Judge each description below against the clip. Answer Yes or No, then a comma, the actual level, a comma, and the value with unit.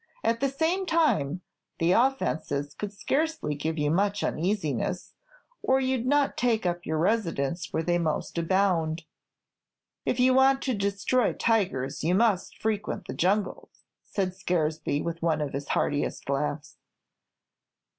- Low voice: No, medium, 185 Hz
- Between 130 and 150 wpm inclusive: Yes, average, 145 wpm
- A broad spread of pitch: Yes, wide, 6.6 semitones